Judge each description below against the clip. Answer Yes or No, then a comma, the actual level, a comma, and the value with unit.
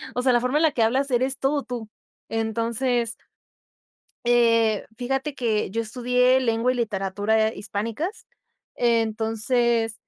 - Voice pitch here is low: No, high, 235 Hz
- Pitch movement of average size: No, narrow, 2.2 semitones